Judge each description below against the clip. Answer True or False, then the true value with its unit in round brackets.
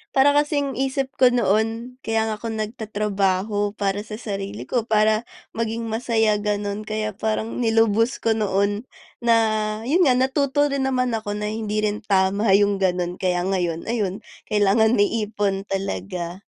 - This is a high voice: True (215 Hz)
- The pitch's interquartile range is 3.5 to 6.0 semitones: False (2.4 semitones)